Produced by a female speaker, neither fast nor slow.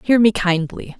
Yes: female; average, 180 wpm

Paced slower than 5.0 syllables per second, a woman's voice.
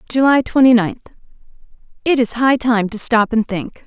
Yes: 4.8 syllables/s; female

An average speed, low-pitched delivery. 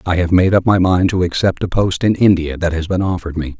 No: fast, 285 wpm; very low, 90 Hz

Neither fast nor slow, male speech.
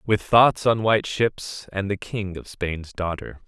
Yes: average, 190 wpm; male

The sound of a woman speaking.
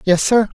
No: male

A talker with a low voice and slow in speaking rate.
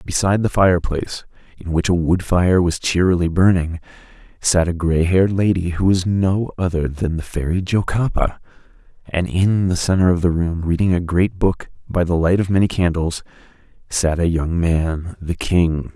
No: very low, 90 Hz; average, 175 wpm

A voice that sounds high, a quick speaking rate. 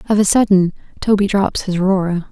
No: high, 195 Hz; average, 180 wpm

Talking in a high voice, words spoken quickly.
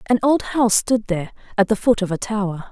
Yes: high, 215 Hz; fast, 245 wpm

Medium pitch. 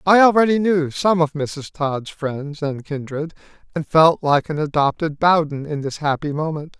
Yes: medium, 155 Hz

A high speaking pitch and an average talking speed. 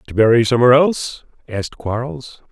No: low, 120 Hz; average, 145 wpm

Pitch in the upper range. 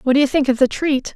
Yes: very high, 270 Hz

